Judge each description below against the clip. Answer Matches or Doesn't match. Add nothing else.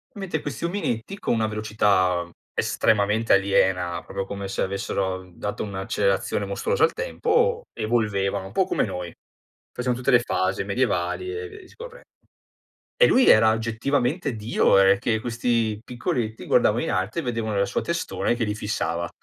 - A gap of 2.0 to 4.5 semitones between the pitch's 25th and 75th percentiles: Doesn't match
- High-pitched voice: Doesn't match